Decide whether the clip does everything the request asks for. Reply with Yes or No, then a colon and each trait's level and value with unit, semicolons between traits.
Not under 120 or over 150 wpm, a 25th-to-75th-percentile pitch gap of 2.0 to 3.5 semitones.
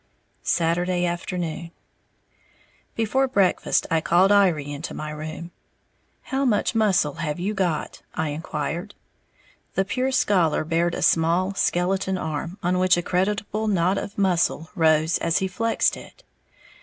Yes: slow, 135 wpm; average, 3.2 semitones